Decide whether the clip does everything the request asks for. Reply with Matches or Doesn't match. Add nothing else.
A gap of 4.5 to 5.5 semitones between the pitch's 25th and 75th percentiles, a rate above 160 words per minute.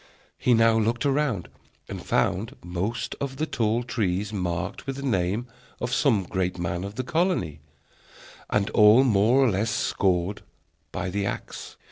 Doesn't match